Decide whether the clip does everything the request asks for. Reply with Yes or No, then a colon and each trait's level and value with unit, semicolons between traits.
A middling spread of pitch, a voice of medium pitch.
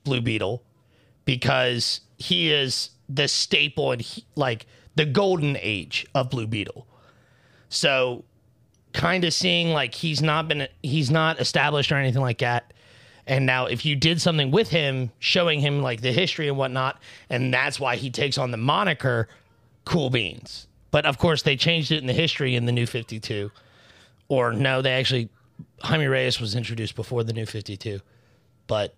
No: average, 3.8 semitones; low, 130 Hz